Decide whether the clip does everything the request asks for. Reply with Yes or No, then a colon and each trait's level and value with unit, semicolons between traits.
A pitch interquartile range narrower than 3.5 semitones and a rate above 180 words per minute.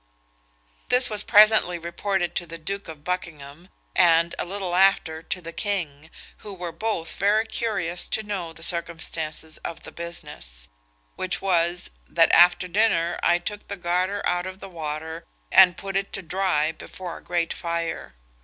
No: average, 2.8 semitones; average, 165 wpm